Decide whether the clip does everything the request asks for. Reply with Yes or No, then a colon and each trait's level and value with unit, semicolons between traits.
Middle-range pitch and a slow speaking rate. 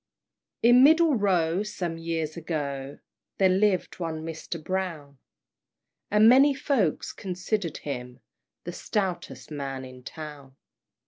Yes: medium, 170 Hz; slow, 115 wpm